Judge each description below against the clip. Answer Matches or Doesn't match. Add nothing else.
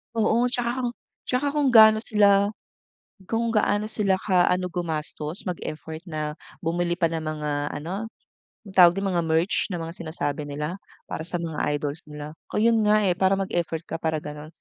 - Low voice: Doesn't match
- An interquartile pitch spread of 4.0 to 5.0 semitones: Matches